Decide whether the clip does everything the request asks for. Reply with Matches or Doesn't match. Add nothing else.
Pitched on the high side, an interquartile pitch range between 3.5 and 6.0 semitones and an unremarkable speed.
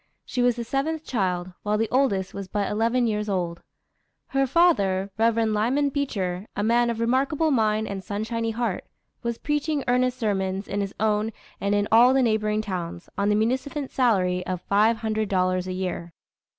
Matches